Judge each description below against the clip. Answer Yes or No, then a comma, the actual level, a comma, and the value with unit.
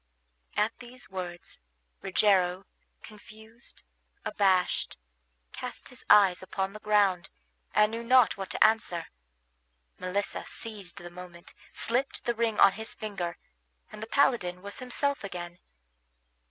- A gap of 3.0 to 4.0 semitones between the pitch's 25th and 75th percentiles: Yes, average, 3.5 semitones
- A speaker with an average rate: No, slow, 125 wpm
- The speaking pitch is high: Yes, high, 200 Hz